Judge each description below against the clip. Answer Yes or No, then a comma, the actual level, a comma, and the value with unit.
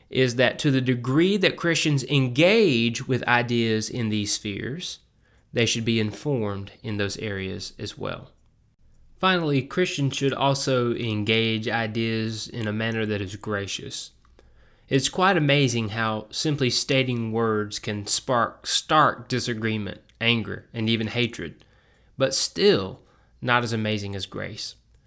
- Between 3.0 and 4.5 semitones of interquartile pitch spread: Yes, average, 3.6 semitones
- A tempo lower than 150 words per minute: Yes, slow, 135 wpm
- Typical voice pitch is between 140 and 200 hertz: No, low, 115 Hz